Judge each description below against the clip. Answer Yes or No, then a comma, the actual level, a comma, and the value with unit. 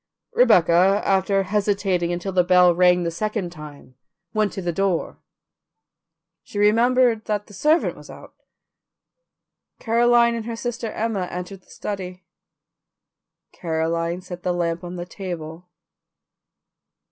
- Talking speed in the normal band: No, slow, 125 wpm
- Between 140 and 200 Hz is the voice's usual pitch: Yes, medium, 185 Hz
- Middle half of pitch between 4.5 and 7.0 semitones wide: No, average, 3.5 semitones